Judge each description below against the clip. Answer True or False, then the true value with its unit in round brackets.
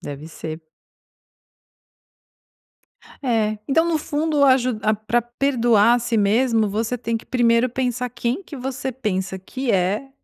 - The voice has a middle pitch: False (240 Hz)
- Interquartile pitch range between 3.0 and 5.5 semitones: True (3.4 semitones)